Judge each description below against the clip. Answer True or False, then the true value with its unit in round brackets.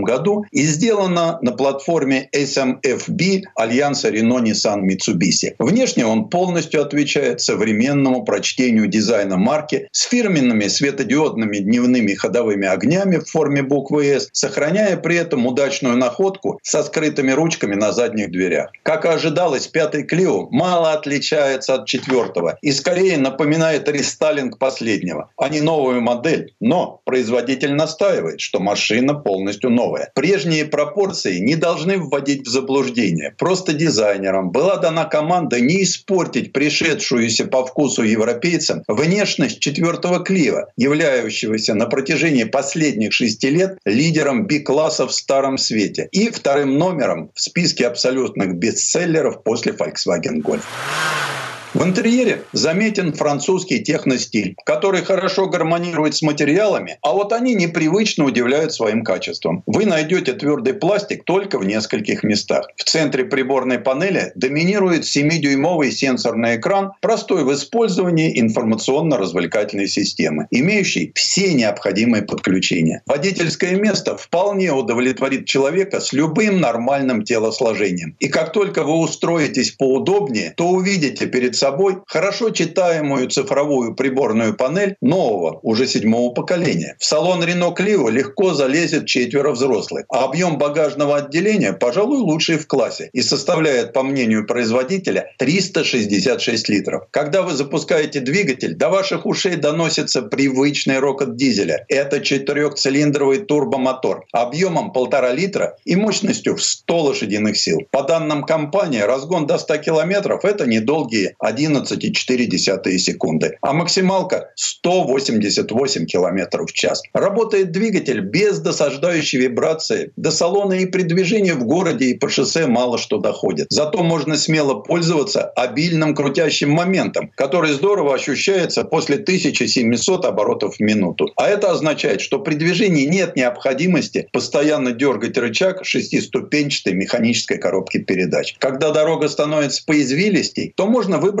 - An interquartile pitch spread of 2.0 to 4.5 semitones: False (5.6 semitones)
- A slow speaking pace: False (125 wpm)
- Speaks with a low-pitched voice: False (150 Hz)